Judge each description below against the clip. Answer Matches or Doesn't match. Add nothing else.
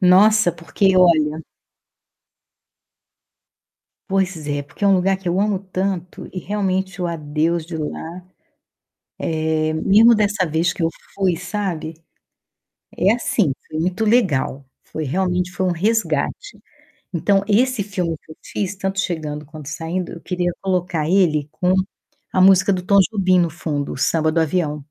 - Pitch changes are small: Doesn't match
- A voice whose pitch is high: Doesn't match